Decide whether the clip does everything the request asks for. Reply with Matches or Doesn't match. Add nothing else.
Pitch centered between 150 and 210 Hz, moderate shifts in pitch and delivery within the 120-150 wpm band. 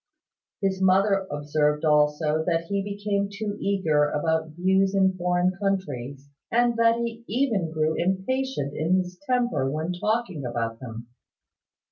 Matches